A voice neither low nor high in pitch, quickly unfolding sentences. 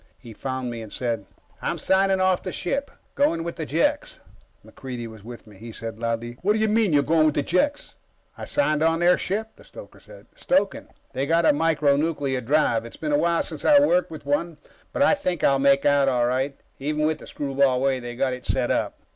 Yes: medium, 145 Hz; fast, 225 wpm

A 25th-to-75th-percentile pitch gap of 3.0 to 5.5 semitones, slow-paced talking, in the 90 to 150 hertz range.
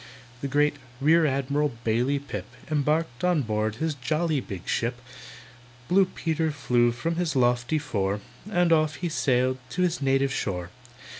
No: average, 4.7 semitones; average, 150 wpm; medium, 140 Hz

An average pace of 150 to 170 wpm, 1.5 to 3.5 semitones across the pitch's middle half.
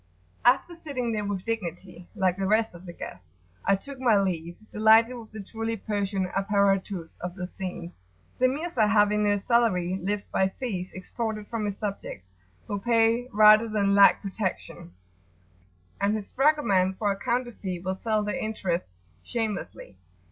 Yes: average, 160 wpm; average, 3.1 semitones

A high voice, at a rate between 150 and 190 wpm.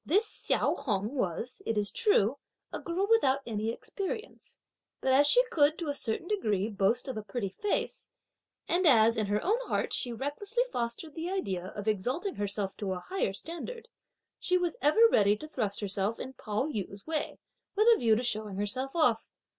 Yes: high, 245 Hz; average, 185 wpm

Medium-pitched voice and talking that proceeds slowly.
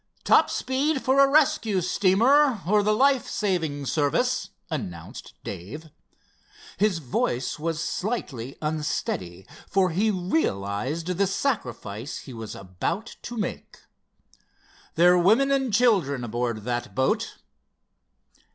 Yes: medium, 175 Hz; slow, 115 wpm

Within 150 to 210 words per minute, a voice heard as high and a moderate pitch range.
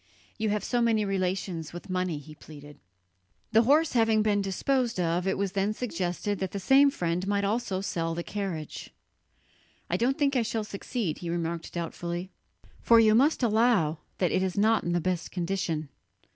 Yes: average, 180 wpm; high, 195 Hz; average, 4.4 semitones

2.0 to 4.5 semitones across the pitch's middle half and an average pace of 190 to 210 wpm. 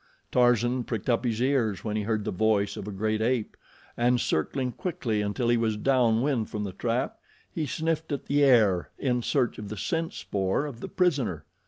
Yes: average, 3.8 semitones; average, 200 wpm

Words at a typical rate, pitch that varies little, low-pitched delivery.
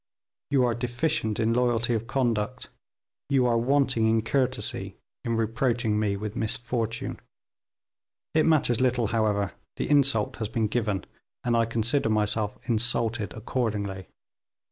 No: slow, 130 wpm; narrow, 2.3 semitones; low, 115 Hz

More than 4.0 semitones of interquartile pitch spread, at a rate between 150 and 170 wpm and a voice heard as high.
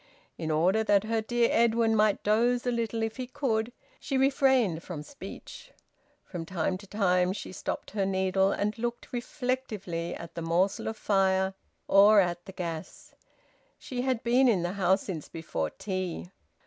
Yes: average, 4.5 semitones; average, 165 wpm; high, 200 Hz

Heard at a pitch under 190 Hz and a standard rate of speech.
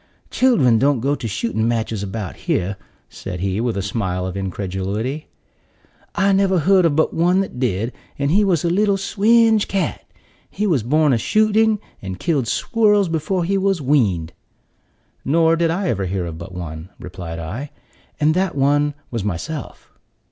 Yes: medium, 140 Hz; average, 170 wpm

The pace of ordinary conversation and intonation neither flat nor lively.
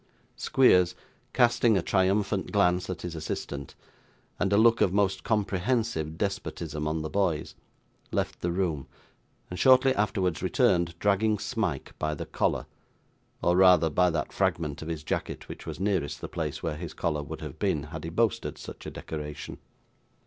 Yes: average, 165 wpm; average, 4.3 semitones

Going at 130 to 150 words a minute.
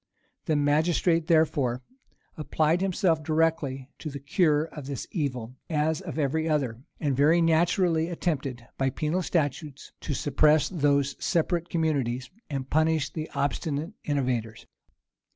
Yes: slow, 135 wpm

